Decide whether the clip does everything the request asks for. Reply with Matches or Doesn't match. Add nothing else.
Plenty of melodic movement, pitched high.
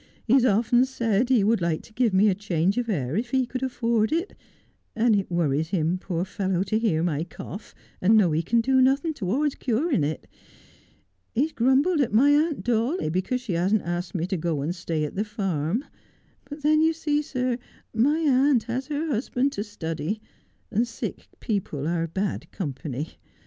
Matches